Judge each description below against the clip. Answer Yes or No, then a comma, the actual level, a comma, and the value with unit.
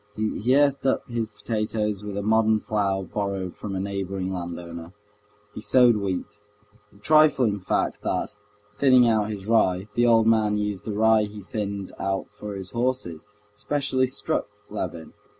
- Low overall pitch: Yes, low, 105 Hz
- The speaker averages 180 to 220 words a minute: No, average, 155 wpm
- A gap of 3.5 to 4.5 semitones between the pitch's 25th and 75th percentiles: No, average, 2.8 semitones